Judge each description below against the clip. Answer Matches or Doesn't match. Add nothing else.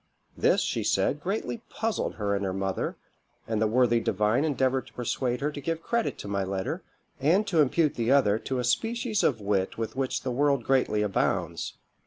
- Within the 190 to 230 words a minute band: Matches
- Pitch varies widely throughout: Matches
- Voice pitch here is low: Matches